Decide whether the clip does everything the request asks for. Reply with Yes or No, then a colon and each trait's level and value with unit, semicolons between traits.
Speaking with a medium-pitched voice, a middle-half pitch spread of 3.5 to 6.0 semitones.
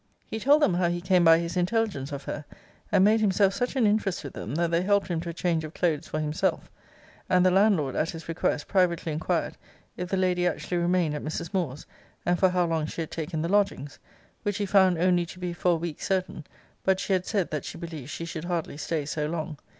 No: medium, 175 Hz; average, 2.8 semitones